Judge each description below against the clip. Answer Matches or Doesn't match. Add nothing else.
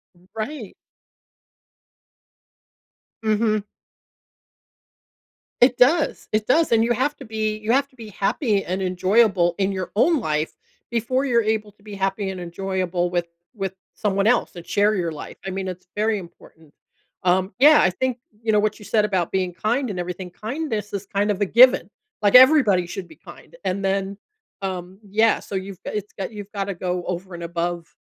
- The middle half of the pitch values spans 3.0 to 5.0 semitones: Matches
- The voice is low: Doesn't match